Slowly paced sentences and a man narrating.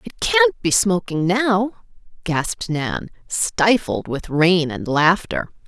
No: slow, 125 wpm; female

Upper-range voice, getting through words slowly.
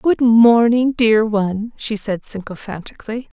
Yes: high, 220 Hz; slow, 125 wpm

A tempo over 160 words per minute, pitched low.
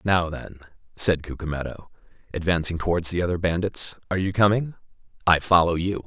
No: average, 140 wpm; very low, 85 Hz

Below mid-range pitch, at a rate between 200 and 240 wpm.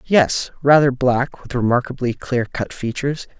No: low, 130 Hz; average, 140 wpm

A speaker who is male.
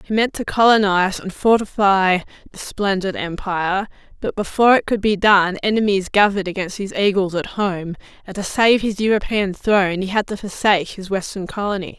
No: female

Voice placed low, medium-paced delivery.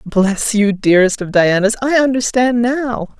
No: high, 220 Hz; average, 150 wpm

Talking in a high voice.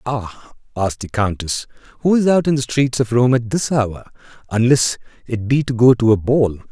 No: low, 120 Hz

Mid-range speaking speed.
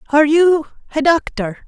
Yes: average, 145 wpm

